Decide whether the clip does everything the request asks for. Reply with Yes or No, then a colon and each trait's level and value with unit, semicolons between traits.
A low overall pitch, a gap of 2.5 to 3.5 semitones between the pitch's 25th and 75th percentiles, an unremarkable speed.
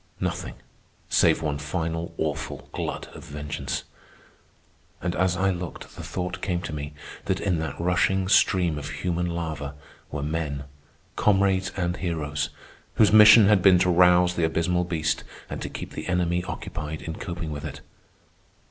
Yes: very low, 85 Hz; average, 2.8 semitones; average, 155 wpm